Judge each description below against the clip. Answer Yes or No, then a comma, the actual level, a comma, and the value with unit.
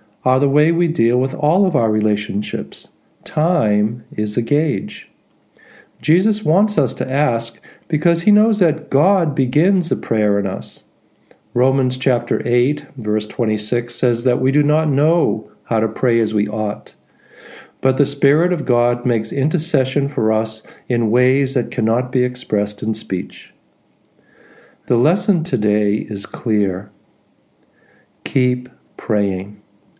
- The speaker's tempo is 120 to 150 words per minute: Yes, average, 140 wpm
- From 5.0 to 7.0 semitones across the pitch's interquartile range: Yes, average, 5.3 semitones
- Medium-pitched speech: No, low, 125 Hz